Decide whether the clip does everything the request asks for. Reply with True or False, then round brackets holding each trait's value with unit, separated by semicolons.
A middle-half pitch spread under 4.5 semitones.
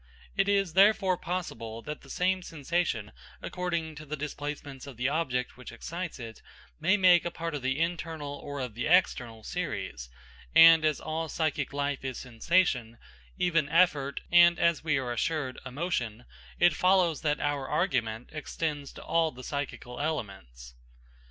False (4.9 semitones)